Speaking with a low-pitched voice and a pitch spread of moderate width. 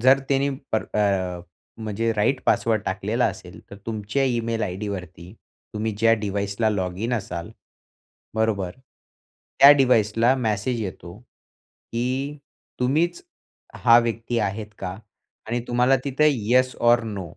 Yes: low, 110 Hz; average, 3.6 semitones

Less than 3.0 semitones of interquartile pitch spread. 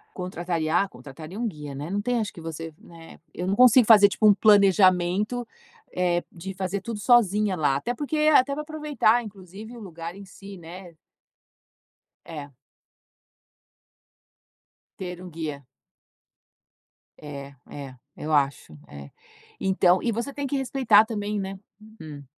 No: average, 5.0 semitones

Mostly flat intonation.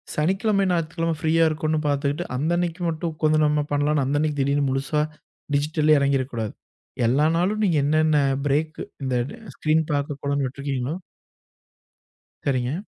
Yes: narrow, 2.3 semitones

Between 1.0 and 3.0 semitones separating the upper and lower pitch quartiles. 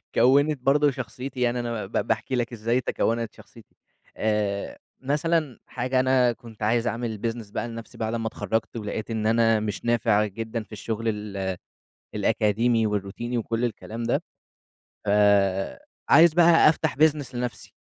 Yes: average, 2.7 semitones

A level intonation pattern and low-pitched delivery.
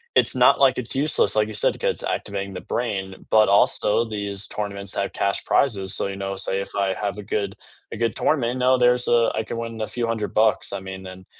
No: average, 3.0 semitones; low, 105 Hz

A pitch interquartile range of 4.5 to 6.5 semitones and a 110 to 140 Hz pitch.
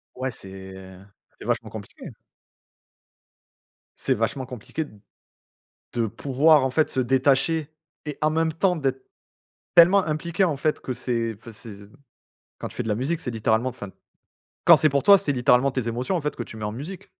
Yes: average, 5.0 semitones; low, 130 Hz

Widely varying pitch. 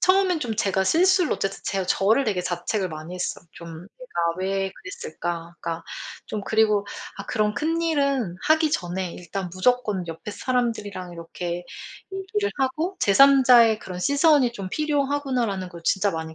Yes: wide, 7.5 semitones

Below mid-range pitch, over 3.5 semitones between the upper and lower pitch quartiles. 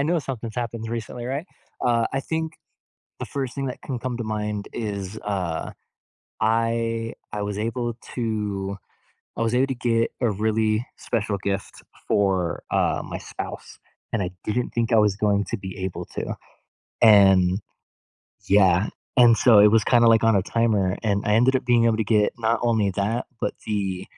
No: low, 110 Hz; narrow, 2.6 semitones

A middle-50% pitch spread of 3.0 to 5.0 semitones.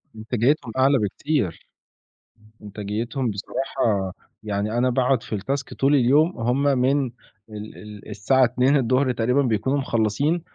Yes: average, 4.1 semitones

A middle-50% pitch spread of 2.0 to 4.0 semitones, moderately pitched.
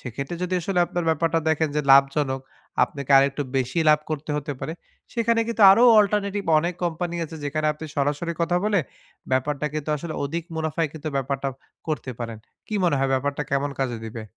Yes: average, 3.7 semitones; medium, 150 Hz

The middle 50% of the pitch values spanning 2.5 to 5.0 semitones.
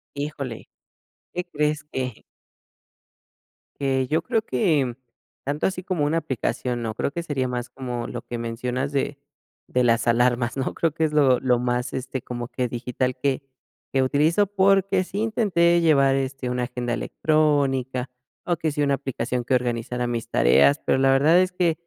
Yes: average, 4.0 semitones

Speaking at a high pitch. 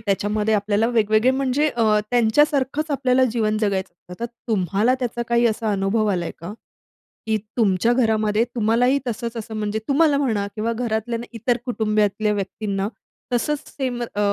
Yes: high, 225 Hz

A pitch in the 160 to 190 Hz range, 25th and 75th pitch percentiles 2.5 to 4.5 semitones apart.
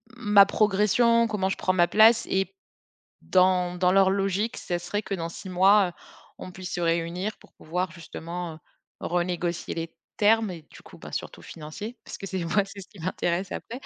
Yes: medium, 185 Hz; average, 2.8 semitones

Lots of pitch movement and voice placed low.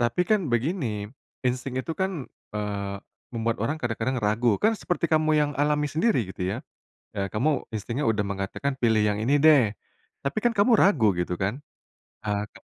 Yes: wide, 6.6 semitones; low, 125 Hz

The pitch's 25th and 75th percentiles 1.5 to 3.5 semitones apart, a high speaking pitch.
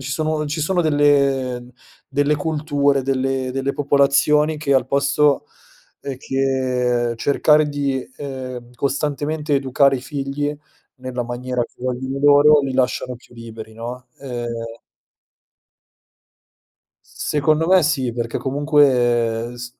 No: narrow, 2.6 semitones; low, 135 Hz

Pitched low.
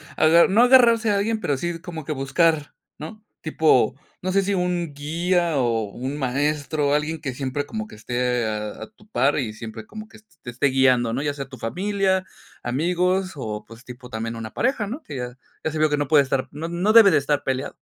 No: medium, 150 Hz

